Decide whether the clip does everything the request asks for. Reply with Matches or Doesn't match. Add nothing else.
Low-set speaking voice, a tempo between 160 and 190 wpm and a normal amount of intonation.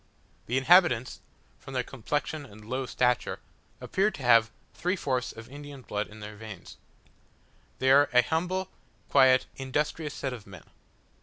Doesn't match